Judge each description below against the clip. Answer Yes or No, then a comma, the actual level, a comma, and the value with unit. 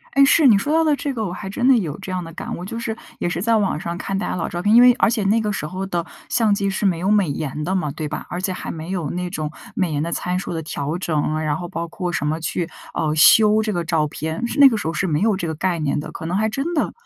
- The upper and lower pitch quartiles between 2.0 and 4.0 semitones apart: No, average, 4.7 semitones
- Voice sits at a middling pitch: Yes, medium, 180 Hz